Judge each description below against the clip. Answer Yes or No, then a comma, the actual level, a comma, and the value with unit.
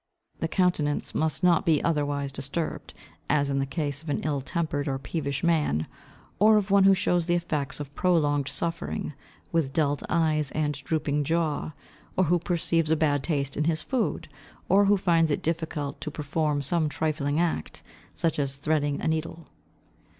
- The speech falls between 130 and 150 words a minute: No, average, 170 wpm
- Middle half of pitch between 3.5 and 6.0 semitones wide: No, average, 2.7 semitones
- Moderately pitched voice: Yes, medium, 155 Hz